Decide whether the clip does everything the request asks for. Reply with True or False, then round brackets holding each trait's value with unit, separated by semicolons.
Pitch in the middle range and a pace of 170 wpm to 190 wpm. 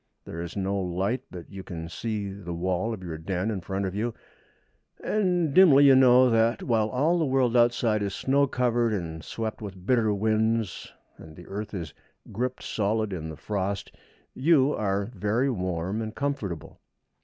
False (105 Hz; 175 wpm)